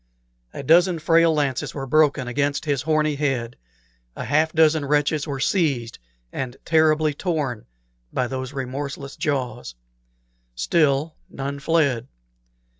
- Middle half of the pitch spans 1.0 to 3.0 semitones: Yes, average, 2.7 semitones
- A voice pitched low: No, medium, 145 Hz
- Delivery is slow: Yes, slow, 120 wpm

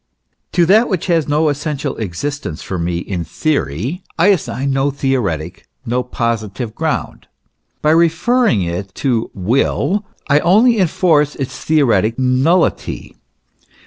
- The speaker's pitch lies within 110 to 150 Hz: Yes, medium, 140 Hz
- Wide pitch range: Yes, wide, 6.9 semitones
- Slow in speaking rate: Yes, slow, 125 wpm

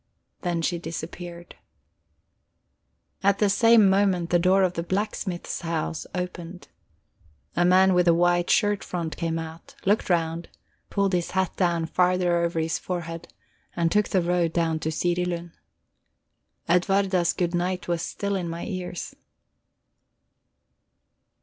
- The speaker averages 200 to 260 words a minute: No, slow, 135 wpm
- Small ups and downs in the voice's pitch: Yes, narrow, 1.8 semitones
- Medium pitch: Yes, medium, 175 Hz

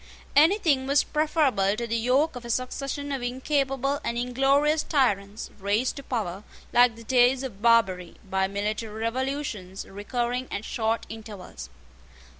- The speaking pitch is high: Yes, high, 245 Hz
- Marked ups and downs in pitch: No, average, 4.4 semitones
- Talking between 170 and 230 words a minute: No, average, 140 wpm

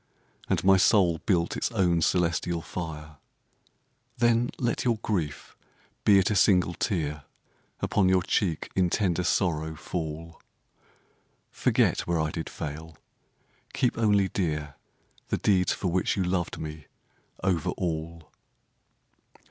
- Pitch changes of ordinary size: Yes, average, 3.3 semitones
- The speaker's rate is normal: No, slow, 125 wpm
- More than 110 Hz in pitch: No, very low, 85 Hz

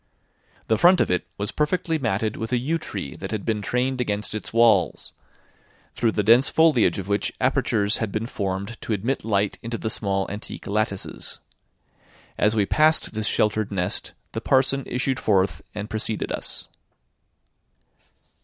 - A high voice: No, low, 110 Hz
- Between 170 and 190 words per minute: No, average, 160 wpm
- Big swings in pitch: No, average, 3.4 semitones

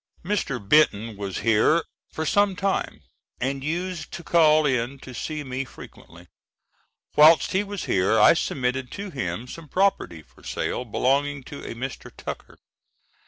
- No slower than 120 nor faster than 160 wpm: Yes, average, 150 wpm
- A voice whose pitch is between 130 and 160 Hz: Yes, medium, 140 Hz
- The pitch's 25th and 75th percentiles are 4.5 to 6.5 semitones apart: Yes, average, 5.1 semitones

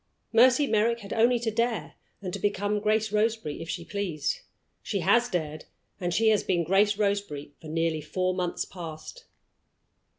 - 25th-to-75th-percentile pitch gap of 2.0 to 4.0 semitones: No, average, 4.7 semitones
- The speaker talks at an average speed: Yes, average, 165 wpm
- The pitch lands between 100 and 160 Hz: No, high, 200 Hz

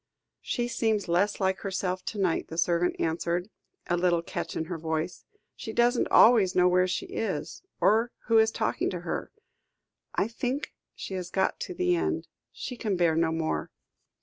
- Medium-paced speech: Yes, average, 175 wpm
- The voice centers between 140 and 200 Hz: Yes, medium, 185 Hz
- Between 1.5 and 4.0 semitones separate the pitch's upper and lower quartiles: No, average, 4.5 semitones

